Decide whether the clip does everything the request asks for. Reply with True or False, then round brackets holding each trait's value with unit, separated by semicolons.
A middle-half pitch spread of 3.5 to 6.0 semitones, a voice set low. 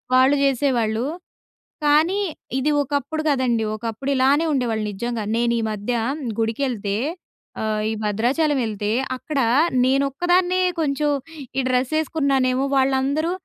False (3.8 semitones; 265 Hz)